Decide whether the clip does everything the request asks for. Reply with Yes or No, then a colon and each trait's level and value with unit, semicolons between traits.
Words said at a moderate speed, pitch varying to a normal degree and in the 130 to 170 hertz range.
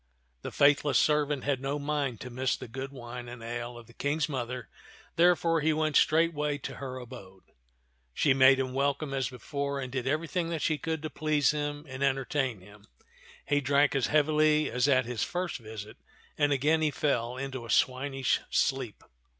Yes: average, 185 wpm; average, 3.0 semitones; low, 135 Hz